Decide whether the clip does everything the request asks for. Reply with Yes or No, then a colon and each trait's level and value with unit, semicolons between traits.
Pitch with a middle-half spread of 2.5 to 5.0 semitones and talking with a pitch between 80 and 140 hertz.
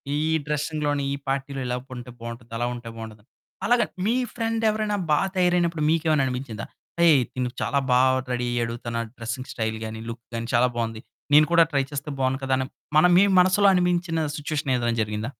No: wide, 5.6 semitones; low, 135 Hz